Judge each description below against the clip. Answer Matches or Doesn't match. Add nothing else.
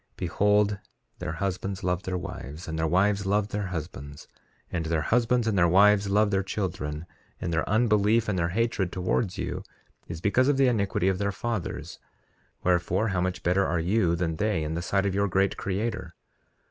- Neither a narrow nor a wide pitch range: Matches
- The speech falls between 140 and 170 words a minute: Doesn't match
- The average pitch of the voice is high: Doesn't match